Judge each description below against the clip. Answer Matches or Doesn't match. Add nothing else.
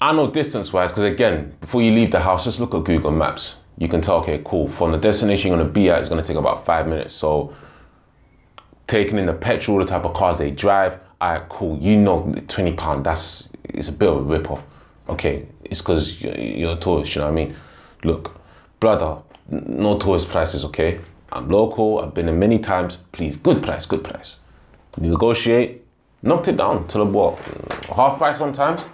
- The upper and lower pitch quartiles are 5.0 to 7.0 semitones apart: Doesn't match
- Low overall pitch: Matches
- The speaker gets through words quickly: Matches